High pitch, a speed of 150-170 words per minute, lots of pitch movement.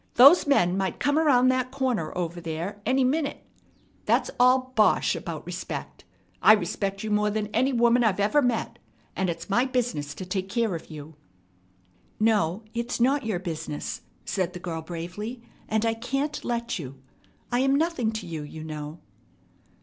Yes: high, 215 Hz; average, 165 wpm; wide, 6.4 semitones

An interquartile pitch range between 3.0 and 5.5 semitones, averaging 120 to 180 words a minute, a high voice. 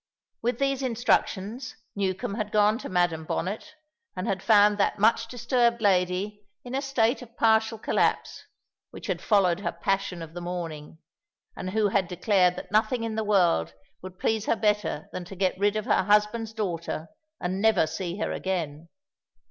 Yes: average, 3.5 semitones; average, 170 wpm; high, 205 Hz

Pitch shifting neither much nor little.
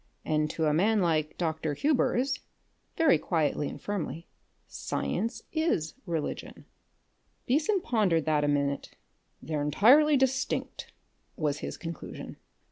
No: wide, 8.6 semitones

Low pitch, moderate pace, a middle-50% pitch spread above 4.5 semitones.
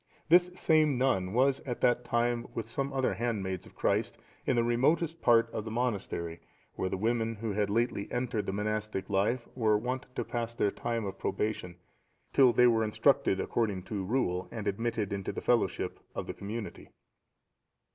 No: low, 115 Hz; average, 175 wpm; average, 3.2 semitones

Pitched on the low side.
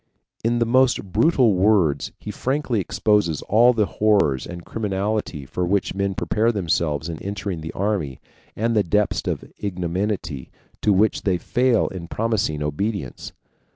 Yes: low, 100 Hz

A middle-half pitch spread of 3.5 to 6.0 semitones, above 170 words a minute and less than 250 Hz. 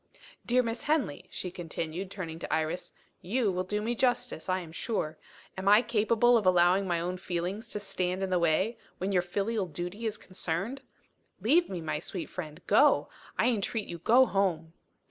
Yes: average, 4.2 semitones; average, 185 wpm; high, 190 Hz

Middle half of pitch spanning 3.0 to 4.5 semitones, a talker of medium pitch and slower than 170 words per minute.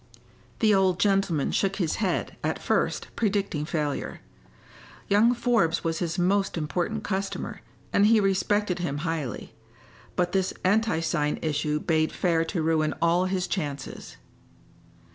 Yes: average, 3.7 semitones; medium, 180 Hz; slow, 135 wpm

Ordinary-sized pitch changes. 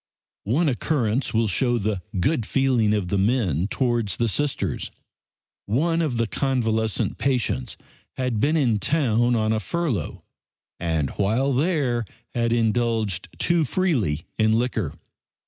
Yes: average, 4.1 semitones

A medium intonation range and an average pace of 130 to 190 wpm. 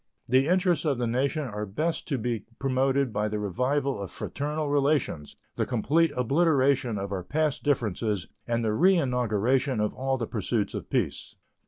Yes: average, 4.9 semitones; average, 165 wpm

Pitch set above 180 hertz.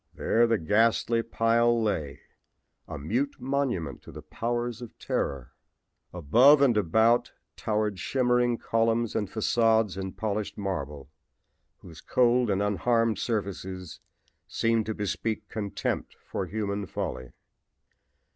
No: low, 110 Hz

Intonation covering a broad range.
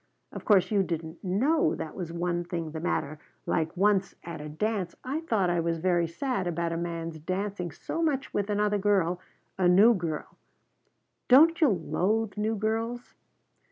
No: average, 4.3 semitones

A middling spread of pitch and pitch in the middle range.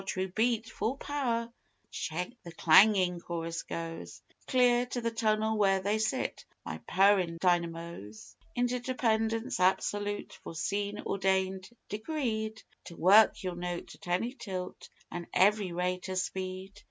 No: average, 3.7 semitones; high, 195 Hz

